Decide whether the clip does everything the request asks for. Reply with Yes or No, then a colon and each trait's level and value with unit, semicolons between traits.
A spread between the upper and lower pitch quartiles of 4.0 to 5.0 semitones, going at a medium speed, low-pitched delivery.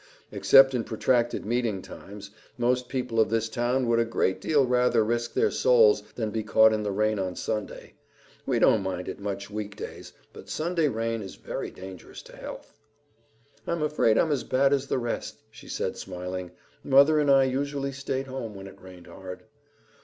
Yes: average, 4.6 semitones; average, 185 wpm; low, 115 Hz